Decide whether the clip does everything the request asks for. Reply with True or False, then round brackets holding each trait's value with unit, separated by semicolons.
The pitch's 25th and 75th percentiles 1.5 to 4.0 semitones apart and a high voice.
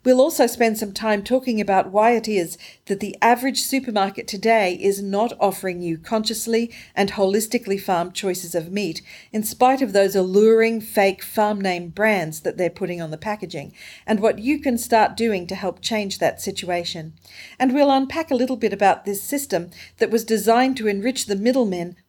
True (3.5 semitones; 210 Hz)